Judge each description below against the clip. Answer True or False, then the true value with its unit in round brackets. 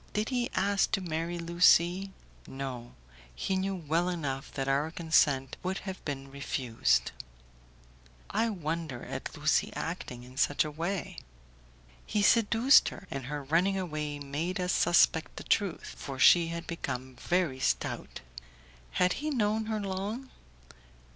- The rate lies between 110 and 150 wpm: True (140 wpm)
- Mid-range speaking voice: True (170 Hz)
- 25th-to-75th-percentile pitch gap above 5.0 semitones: True (5.5 semitones)